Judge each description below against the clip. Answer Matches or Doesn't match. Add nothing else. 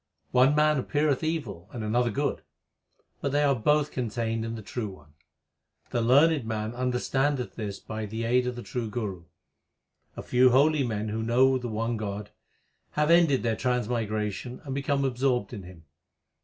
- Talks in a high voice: Doesn't match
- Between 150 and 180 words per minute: Matches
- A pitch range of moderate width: Matches